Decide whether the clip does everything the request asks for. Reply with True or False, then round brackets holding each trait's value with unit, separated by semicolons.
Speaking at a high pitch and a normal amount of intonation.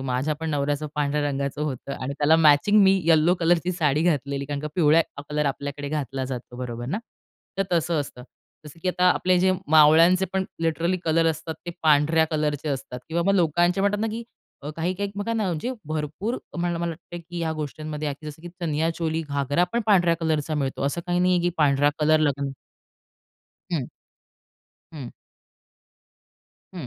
False (155 Hz; 3.2 semitones)